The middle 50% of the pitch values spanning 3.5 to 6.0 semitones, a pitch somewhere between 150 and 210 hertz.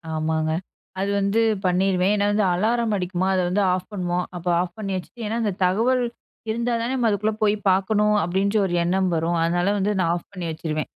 No: average, 3.0 semitones; high, 190 Hz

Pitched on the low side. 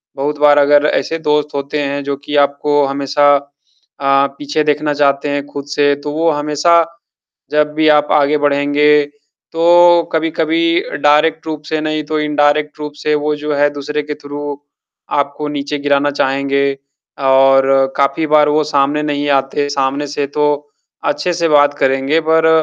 No: medium, 145 Hz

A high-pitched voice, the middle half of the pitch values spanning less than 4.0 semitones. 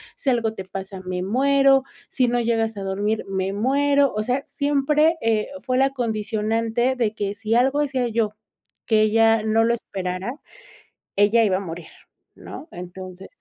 No: high, 225 Hz; average, 4.3 semitones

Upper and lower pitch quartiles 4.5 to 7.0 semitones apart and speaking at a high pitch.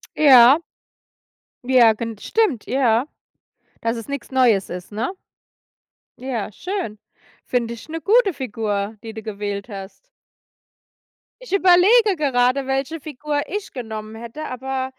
Yes: average, 5.2 semitones; very high, 250 Hz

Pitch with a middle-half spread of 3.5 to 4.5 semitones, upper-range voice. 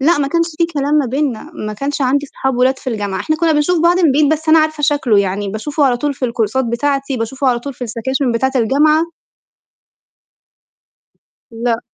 Yes: average, 4.1 semitones; very high, 275 Hz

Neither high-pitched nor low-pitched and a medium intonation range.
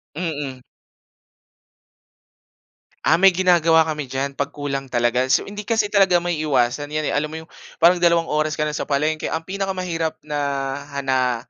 Yes: medium, 155 Hz; average, 3.8 semitones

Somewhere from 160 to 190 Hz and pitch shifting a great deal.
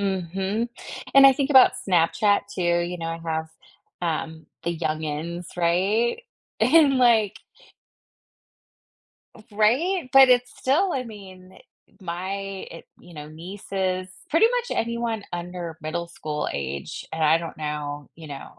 Yes: medium, 185 Hz; wide, 6.3 semitones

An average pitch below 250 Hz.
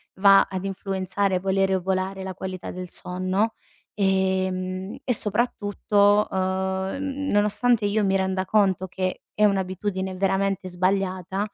Yes: high, 190 Hz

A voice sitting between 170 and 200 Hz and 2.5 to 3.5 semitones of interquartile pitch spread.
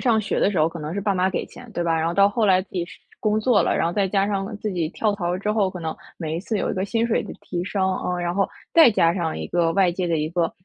Yes: medium, 185 Hz; average, 3.1 semitones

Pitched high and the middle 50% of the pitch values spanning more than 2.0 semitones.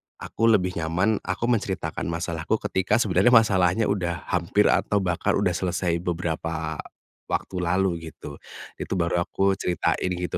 No: very low, 90 Hz; narrow, 2.4 semitones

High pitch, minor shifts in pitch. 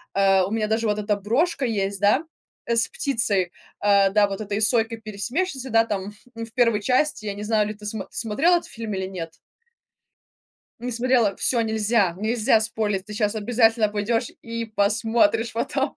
Yes: high, 220 Hz; narrow, 2.2 semitones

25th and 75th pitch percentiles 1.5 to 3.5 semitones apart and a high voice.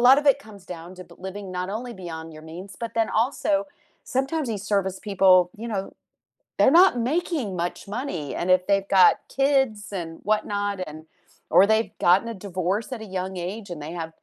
No: average, 4.3 semitones; high, 200 Hz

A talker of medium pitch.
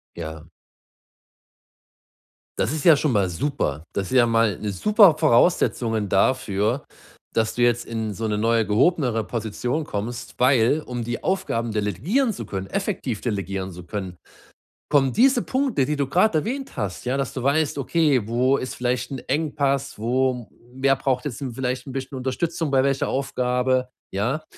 No: low, 125 Hz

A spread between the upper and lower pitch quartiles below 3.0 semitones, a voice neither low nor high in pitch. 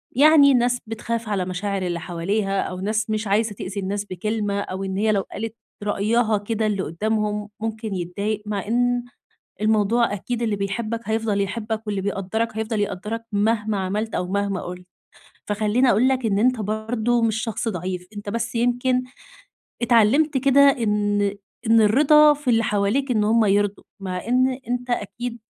No: narrow, 2.6 semitones; high, 215 Hz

